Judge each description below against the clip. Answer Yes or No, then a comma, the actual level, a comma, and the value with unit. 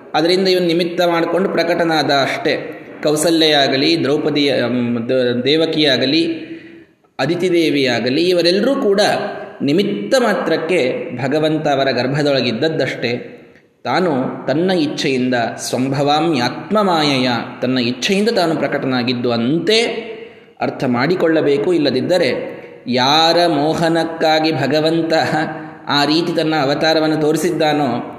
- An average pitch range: Yes, average, 3.7 semitones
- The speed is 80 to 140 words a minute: Yes, average, 85 wpm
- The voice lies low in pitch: No, medium, 155 Hz